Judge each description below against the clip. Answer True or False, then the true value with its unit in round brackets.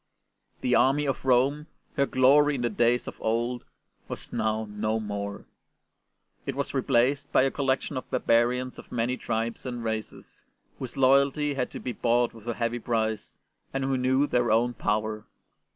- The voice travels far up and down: False (2.8 semitones)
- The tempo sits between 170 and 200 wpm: True (180 wpm)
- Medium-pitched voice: False (120 Hz)